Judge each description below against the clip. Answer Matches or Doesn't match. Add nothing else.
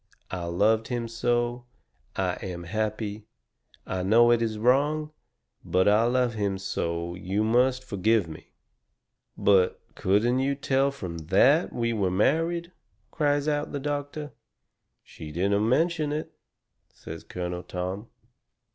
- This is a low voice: Matches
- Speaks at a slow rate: Matches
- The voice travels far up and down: Matches